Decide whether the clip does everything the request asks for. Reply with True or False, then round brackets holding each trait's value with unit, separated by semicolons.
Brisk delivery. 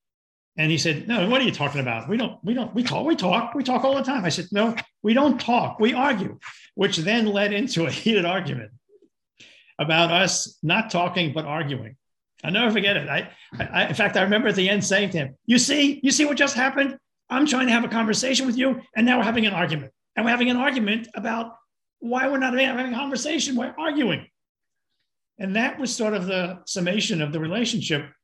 True (220 wpm)